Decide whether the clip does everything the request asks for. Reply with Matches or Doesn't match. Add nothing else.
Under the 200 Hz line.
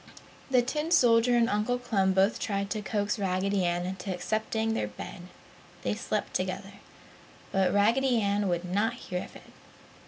Doesn't match